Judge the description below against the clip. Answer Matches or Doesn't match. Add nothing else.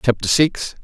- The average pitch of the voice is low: Matches